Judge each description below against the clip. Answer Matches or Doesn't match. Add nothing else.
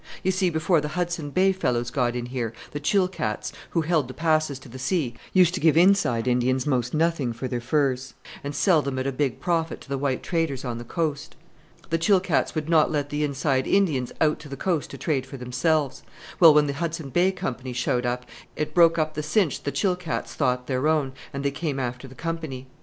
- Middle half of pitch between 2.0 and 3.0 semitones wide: Doesn't match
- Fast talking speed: Matches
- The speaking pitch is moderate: Matches